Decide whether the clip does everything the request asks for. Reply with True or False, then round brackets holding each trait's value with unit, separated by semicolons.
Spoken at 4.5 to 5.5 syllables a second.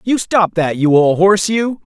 True (5.2 syllables/s)